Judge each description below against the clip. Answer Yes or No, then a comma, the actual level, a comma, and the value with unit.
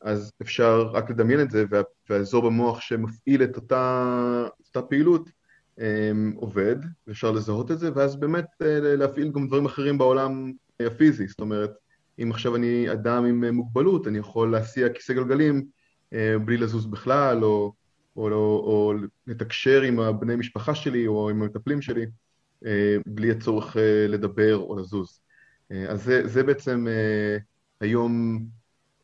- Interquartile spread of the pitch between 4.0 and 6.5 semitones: No, average, 3.6 semitones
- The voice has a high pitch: No, low, 115 Hz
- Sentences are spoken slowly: No, average, 135 wpm